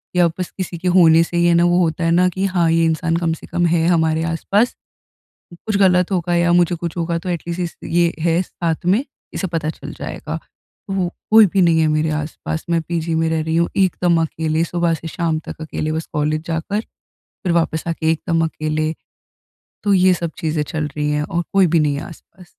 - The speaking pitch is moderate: Yes, medium, 170 Hz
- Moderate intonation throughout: No, narrow, 1.7 semitones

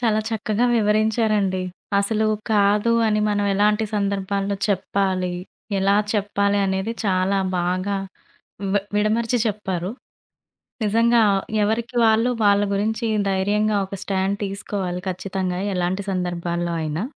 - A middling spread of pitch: No, narrow, 2.1 semitones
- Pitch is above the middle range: Yes, high, 200 Hz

